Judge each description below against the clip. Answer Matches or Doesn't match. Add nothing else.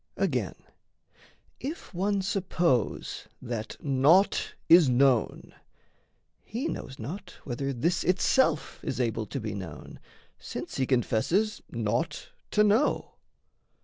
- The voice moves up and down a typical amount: Doesn't match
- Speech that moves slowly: Matches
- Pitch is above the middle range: Doesn't match